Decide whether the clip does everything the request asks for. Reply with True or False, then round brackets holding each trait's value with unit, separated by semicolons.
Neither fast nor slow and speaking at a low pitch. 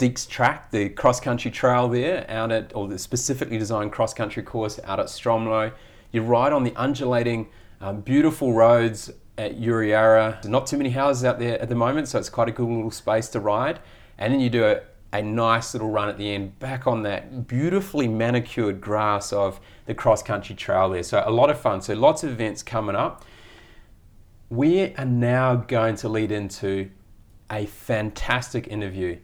True (185 wpm; 115 Hz)